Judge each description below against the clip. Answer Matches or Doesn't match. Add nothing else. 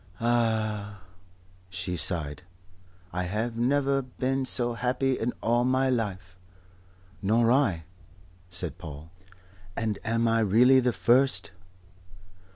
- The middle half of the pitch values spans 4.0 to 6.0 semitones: Matches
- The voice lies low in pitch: Matches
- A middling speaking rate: Doesn't match